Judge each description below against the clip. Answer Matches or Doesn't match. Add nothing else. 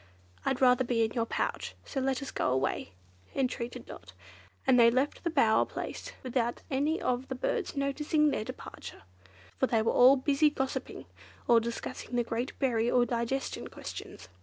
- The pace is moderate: Matches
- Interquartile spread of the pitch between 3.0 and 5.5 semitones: Doesn't match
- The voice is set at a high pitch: Matches